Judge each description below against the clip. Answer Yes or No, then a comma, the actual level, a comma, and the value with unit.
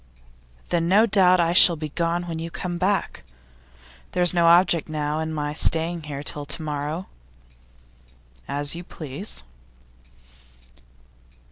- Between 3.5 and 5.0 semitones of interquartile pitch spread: No, narrow, 2.6 semitones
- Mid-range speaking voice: Yes, medium, 165 Hz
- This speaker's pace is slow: Yes, slow, 130 wpm